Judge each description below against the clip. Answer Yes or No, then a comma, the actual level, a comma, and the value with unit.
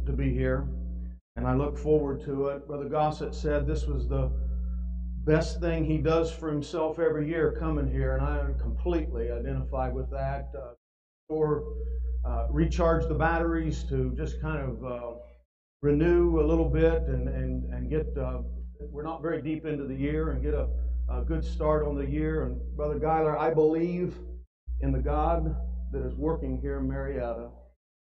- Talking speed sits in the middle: Yes, average, 175 wpm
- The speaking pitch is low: Yes, very low, 75 Hz